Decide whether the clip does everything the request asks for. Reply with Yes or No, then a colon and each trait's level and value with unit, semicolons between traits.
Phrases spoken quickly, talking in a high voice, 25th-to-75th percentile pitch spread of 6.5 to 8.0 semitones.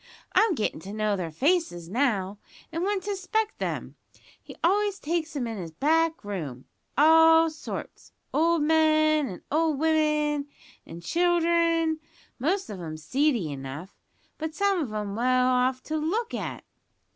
No: average, 150 wpm; very high, 305 Hz; wide, 7.7 semitones